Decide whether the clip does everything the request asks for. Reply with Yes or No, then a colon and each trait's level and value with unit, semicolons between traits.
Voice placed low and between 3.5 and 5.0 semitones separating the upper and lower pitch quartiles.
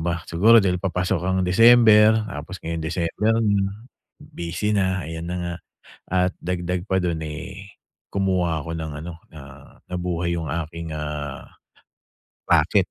No: very low, 90 Hz; average, 2.8 semitones